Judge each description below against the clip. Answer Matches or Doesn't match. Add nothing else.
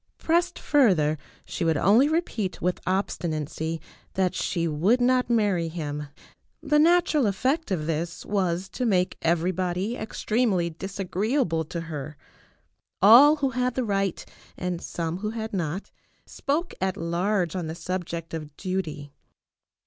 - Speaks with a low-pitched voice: Doesn't match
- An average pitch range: Doesn't match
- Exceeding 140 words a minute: Doesn't match